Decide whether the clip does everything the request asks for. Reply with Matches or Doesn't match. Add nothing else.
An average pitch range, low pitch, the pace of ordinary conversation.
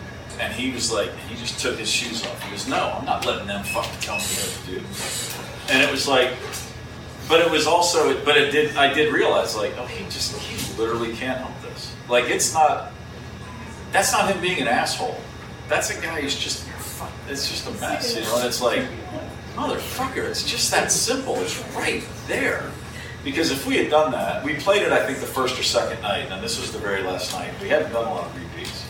Doesn't match